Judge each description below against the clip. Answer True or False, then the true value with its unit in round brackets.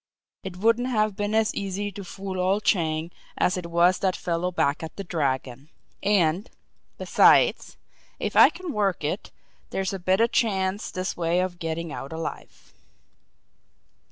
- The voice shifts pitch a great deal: False (3.3 semitones)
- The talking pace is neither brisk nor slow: True (155 wpm)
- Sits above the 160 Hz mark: True (185 Hz)